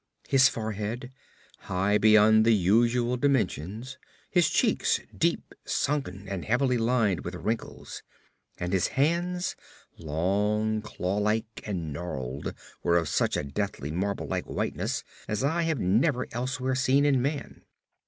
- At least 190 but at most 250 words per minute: No, slow, 135 wpm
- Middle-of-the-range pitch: No, low, 110 Hz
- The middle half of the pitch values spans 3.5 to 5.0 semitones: No, wide, 5.4 semitones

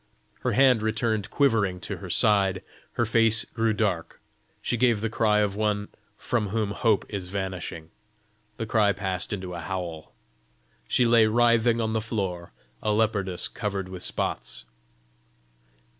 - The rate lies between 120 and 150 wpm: Yes, average, 145 wpm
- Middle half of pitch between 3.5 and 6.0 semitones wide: No, average, 2.9 semitones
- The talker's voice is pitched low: Yes, low, 105 Hz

